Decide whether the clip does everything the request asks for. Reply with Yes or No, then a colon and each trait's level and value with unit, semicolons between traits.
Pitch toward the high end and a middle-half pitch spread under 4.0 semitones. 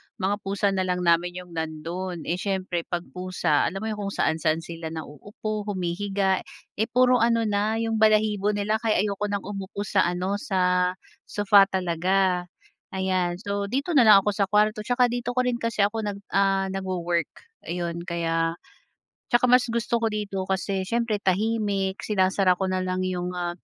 Yes: high, 195 Hz; average, 2.8 semitones